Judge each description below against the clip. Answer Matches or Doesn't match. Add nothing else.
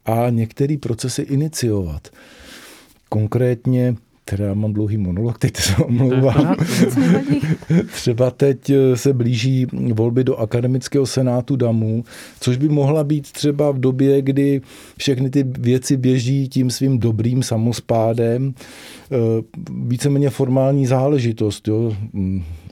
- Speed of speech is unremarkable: Doesn't match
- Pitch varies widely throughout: Doesn't match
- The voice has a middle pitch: Doesn't match